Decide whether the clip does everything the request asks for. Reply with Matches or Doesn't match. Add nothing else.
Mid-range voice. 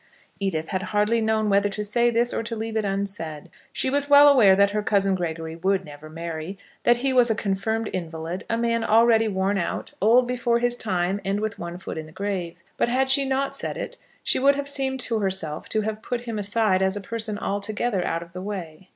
Doesn't match